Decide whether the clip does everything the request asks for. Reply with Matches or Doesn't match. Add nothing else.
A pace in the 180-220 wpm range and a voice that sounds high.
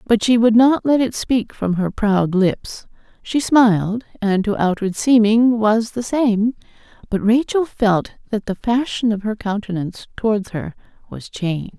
Doesn't match